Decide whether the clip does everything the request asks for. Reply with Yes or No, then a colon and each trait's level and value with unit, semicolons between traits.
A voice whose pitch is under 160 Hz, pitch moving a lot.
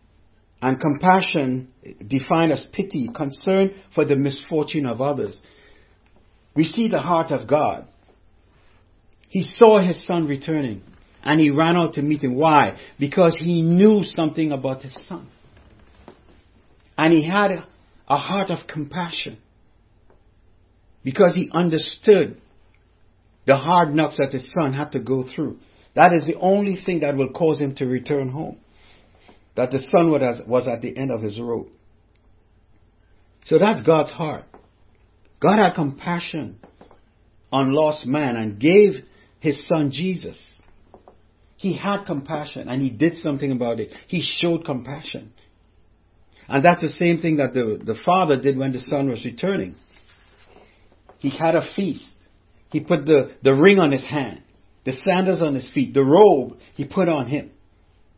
Yes: medium, 140 Hz; wide, 7.5 semitones